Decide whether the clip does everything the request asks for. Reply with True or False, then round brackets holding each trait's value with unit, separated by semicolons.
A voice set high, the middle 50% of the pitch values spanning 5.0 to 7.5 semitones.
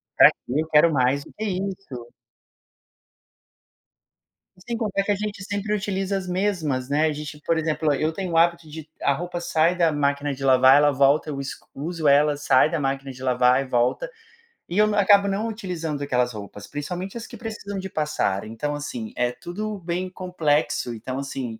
False (155 Hz; 5.6 semitones)